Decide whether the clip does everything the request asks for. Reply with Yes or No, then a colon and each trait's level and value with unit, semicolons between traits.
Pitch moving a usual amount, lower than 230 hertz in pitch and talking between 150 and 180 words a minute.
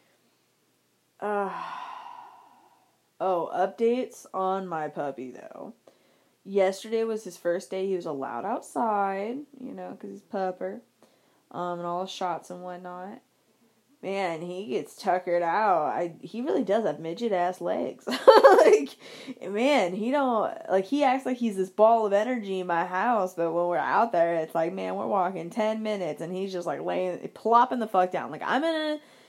Yes: average, 4.6 semitones; high, 190 Hz; average, 170 wpm